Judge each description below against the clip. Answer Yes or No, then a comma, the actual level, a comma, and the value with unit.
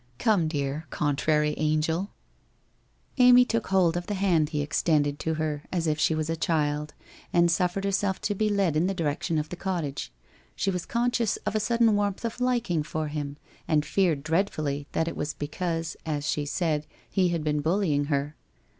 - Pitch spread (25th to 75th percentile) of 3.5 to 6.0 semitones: Yes, average, 4.4 semitones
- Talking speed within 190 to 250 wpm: Yes, average, 200 wpm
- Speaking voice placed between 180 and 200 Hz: No, medium, 165 Hz